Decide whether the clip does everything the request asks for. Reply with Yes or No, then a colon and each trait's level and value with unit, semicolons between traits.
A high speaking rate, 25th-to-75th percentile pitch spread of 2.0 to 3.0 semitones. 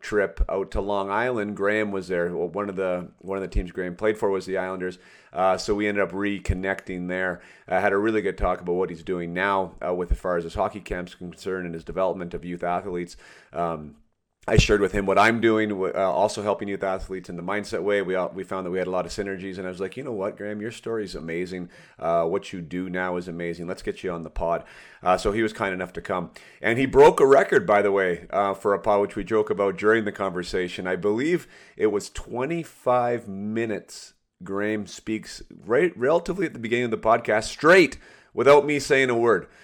Yes: fast, 240 wpm; narrow, 2.5 semitones